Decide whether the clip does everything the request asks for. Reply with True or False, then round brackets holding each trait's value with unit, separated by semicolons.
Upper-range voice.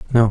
False (115 Hz)